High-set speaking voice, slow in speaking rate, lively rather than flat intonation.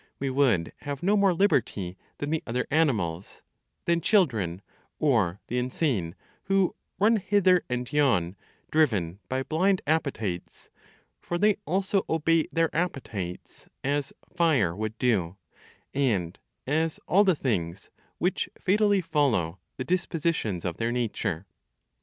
No: medium, 140 Hz; slow, 130 wpm; wide, 8.9 semitones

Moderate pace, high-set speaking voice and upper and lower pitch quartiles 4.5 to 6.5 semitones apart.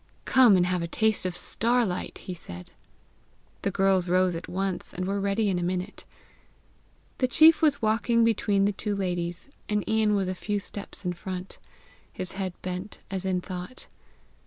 No: average, 180 wpm; high, 195 Hz; average, 2.7 semitones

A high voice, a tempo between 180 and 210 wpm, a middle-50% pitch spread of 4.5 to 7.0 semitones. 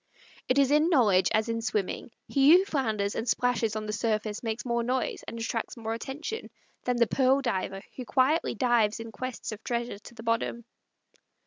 No: high, 235 Hz; average, 190 wpm; average, 2.8 semitones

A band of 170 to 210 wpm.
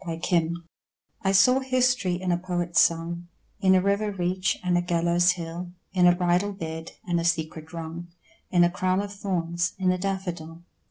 Yes: average, 175 wpm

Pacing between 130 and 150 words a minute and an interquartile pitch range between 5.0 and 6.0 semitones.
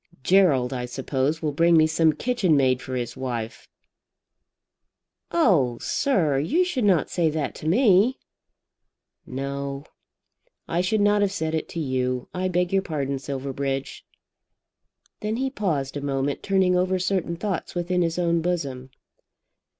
Yes: average, 145 wpm; wide, 5.4 semitones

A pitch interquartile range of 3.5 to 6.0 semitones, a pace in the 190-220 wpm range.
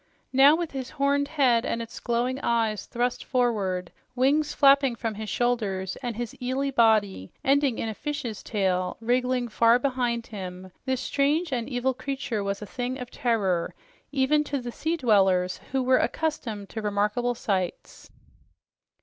No: average, 4.0 semitones; average, 160 wpm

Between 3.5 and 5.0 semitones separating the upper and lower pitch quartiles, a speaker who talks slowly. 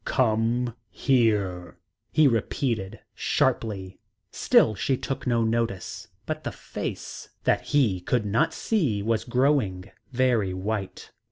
Yes: average, 4.4 semitones; slow, 115 wpm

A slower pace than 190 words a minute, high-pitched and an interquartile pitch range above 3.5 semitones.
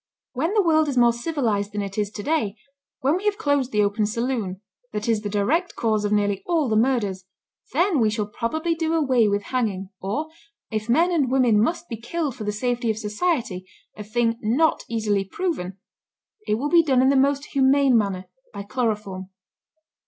No: average, 195 wpm; high, 235 Hz; wide, 5.5 semitones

